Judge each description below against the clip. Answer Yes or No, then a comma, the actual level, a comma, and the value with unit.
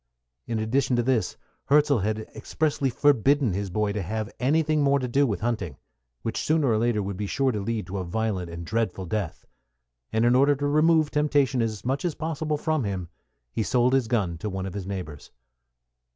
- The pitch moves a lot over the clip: Yes, wide, 5.7 semitones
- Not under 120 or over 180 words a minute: No, average, 200 wpm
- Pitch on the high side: No, low, 115 Hz